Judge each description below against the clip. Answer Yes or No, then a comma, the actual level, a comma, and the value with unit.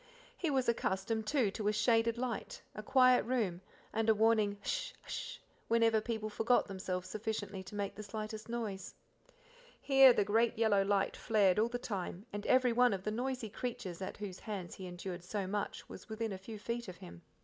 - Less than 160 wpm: No, average, 195 wpm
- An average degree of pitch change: Yes, average, 3.0 semitones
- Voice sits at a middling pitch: No, high, 215 Hz